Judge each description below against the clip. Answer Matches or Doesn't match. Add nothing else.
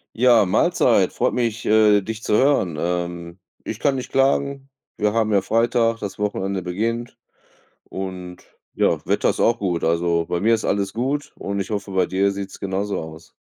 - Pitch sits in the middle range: Doesn't match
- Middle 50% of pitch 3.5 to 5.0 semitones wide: Matches